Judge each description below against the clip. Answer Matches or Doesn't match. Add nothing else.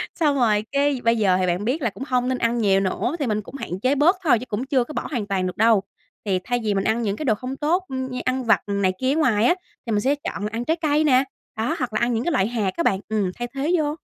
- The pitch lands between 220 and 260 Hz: Matches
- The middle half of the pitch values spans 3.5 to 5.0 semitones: Matches